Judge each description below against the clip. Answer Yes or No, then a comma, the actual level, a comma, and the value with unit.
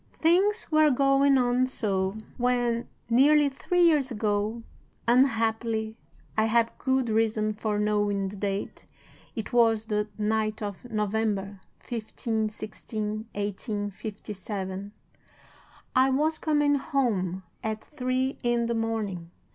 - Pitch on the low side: No, high, 225 Hz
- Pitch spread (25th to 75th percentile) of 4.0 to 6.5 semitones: No, average, 3.6 semitones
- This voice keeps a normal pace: No, slow, 115 wpm